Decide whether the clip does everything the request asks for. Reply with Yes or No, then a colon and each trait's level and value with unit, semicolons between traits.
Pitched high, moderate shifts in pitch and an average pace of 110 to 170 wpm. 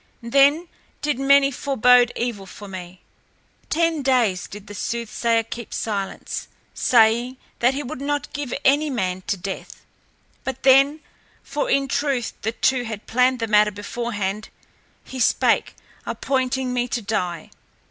Yes: high, 245 Hz; average, 4.5 semitones; average, 140 wpm